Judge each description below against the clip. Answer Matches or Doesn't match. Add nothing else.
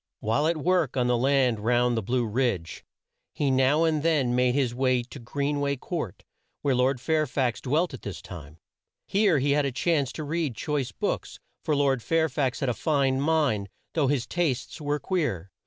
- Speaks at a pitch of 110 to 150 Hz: Matches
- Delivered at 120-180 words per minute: Doesn't match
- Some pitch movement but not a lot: Matches